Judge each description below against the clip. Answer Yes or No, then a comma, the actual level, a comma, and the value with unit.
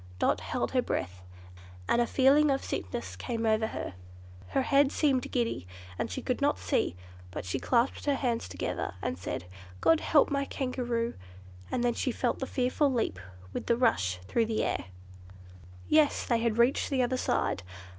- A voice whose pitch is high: Yes, high, 240 Hz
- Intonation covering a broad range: No, average, 3.5 semitones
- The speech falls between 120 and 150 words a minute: No, average, 175 wpm